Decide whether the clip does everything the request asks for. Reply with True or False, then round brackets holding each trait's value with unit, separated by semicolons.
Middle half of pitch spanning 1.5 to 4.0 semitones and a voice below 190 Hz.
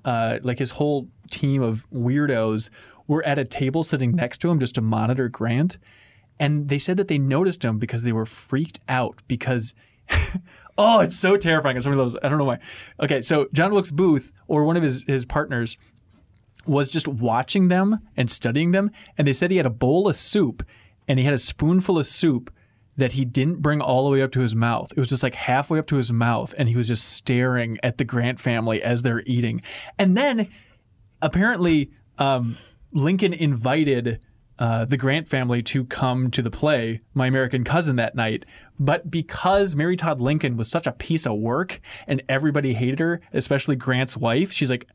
False (4.4 semitones; 135 Hz)